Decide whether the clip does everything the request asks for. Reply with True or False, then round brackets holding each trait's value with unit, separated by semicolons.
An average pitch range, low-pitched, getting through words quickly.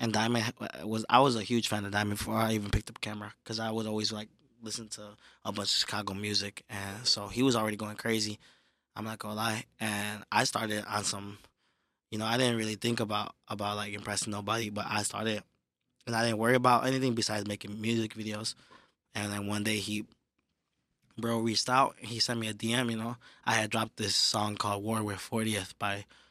False (1.6 semitones; 110 Hz; 215 wpm)